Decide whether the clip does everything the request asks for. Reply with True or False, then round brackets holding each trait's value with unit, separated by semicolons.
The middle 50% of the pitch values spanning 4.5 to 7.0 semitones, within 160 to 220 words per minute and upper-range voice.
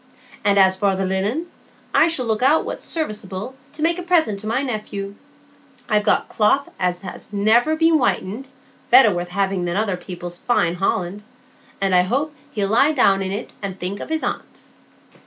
True (5.5 semitones; 190 wpm; 205 Hz)